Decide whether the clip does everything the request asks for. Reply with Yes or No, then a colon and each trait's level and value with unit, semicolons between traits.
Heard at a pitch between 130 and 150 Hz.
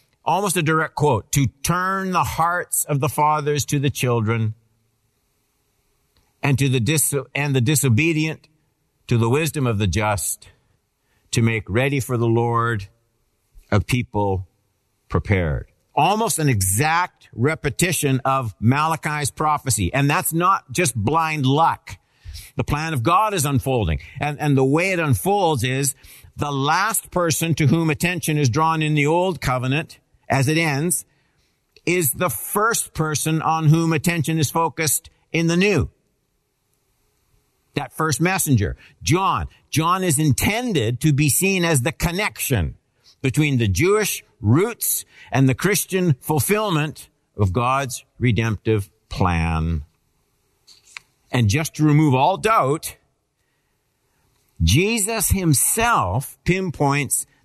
Yes: medium, 140 Hz